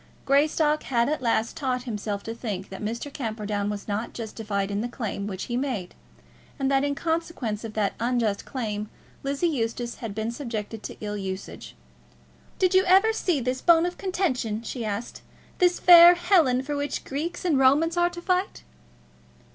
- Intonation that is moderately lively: No, wide, 6.5 semitones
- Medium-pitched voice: No, very high, 250 Hz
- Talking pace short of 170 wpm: No, average, 175 wpm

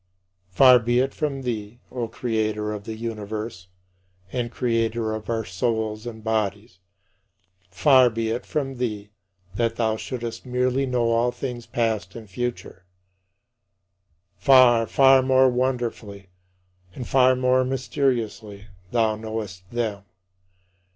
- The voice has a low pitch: Yes, low, 115 Hz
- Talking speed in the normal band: No, slow, 125 wpm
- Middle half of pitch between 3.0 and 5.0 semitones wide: No, narrow, 2.6 semitones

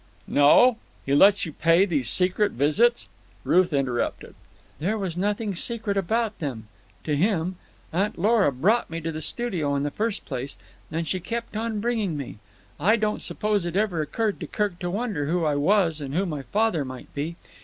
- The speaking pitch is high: No, medium, 180 Hz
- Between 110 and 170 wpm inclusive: No, average, 180 wpm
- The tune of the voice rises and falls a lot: Yes, wide, 5.9 semitones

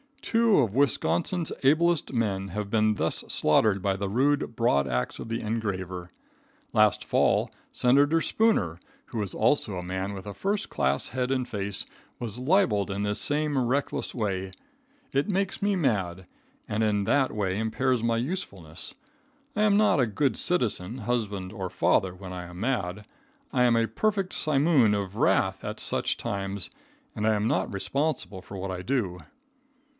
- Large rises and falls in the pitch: Yes, wide, 6.0 semitones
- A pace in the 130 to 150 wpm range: No, average, 165 wpm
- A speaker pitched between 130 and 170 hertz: No, low, 110 Hz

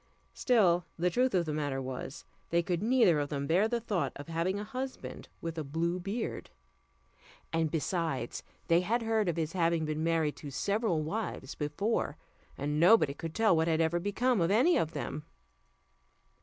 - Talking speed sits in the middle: Yes, average, 180 wpm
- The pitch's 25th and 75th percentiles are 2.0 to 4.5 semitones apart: No, average, 5.1 semitones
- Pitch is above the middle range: No, medium, 170 Hz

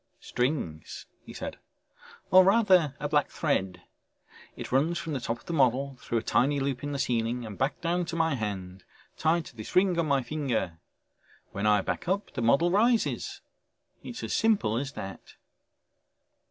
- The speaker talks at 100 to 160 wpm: No, average, 175 wpm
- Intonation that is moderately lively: No, wide, 6.5 semitones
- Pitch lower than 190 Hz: Yes, medium, 140 Hz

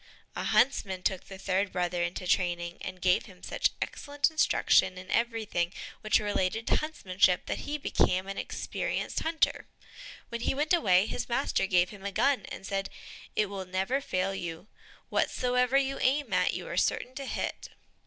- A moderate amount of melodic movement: No, wide, 5.8 semitones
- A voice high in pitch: Yes, high, 195 Hz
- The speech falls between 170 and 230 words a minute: Yes, average, 175 wpm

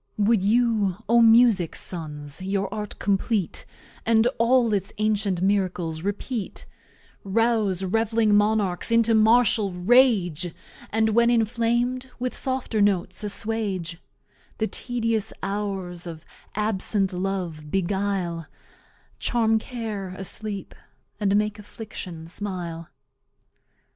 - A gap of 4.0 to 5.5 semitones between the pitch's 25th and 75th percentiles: No, average, 3.3 semitones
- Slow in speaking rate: Yes, slow, 105 wpm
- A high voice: Yes, high, 205 Hz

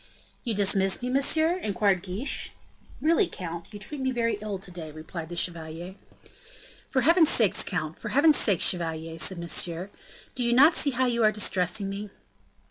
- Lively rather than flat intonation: Yes, wide, 6.4 semitones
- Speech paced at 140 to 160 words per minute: No, average, 175 wpm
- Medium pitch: No, high, 200 Hz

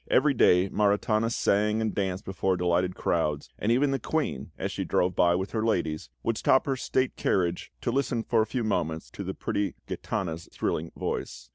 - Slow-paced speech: No, average, 190 wpm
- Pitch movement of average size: Yes, average, 4.6 semitones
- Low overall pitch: Yes, low, 100 Hz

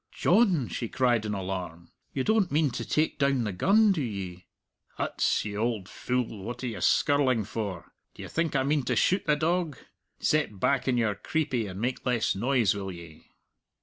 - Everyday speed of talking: Yes, average, 185 wpm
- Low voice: Yes, low, 120 Hz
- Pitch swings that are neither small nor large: No, wide, 6.3 semitones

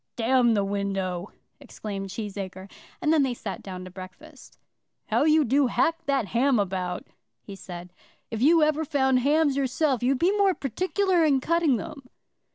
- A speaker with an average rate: Yes, average, 165 wpm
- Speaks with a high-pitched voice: Yes, very high, 260 Hz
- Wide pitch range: Yes, wide, 7.6 semitones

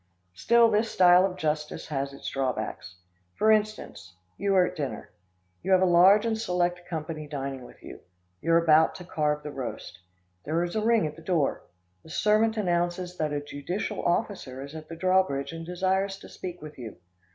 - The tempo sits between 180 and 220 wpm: Yes, average, 190 wpm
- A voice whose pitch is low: No, medium, 175 Hz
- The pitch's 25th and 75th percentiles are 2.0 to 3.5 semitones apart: No, average, 4.2 semitones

